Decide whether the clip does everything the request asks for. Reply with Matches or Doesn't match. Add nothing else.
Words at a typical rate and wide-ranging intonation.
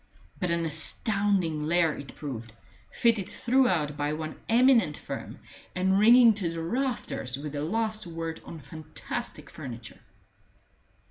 Doesn't match